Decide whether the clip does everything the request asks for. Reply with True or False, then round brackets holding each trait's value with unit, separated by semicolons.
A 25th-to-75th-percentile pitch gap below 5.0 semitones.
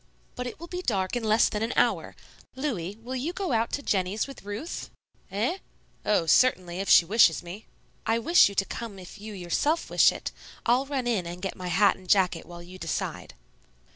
False (5.3 semitones)